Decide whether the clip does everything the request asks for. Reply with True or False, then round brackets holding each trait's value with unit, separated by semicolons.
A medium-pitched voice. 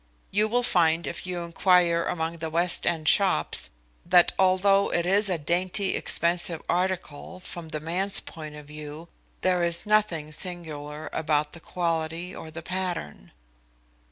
True (170 Hz)